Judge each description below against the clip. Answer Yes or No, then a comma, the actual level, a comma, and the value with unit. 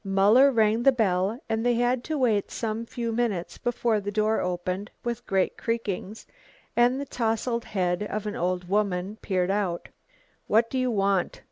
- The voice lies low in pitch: No, high, 215 Hz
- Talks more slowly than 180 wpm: Yes, average, 170 wpm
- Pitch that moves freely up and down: No, average, 3.5 semitones